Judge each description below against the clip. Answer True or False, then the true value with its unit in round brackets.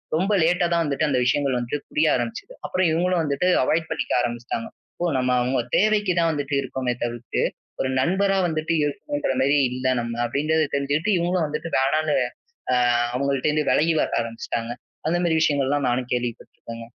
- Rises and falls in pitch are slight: False (4.7 semitones)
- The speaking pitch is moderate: True (145 Hz)